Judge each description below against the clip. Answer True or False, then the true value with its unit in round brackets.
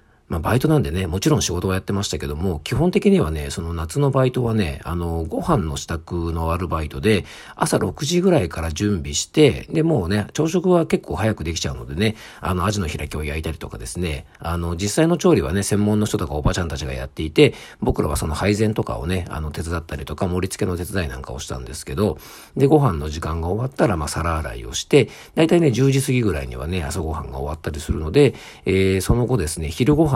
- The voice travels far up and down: True (6.9 semitones)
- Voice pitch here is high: False (90 Hz)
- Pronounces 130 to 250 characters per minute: False (445 characters per minute)